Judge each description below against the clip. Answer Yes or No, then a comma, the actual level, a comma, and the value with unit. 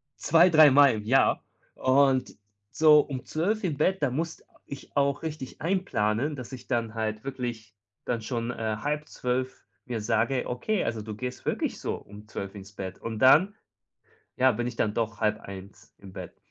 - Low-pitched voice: Yes, low, 125 Hz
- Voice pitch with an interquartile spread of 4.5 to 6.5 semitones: Yes, average, 4.8 semitones